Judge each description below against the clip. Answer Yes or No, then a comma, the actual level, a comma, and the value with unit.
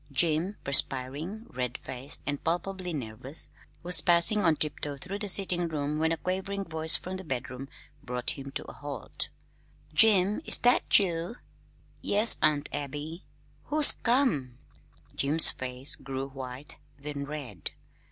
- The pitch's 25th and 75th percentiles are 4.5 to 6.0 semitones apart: Yes, average, 5.2 semitones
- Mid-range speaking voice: Yes, medium, 155 Hz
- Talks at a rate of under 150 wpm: Yes, average, 140 wpm